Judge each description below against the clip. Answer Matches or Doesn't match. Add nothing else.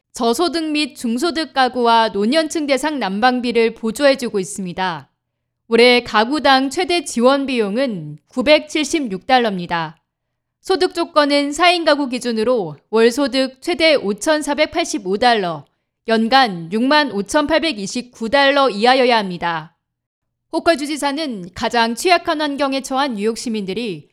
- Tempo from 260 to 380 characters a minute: Doesn't match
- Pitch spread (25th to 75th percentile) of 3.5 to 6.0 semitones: Matches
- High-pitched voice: Matches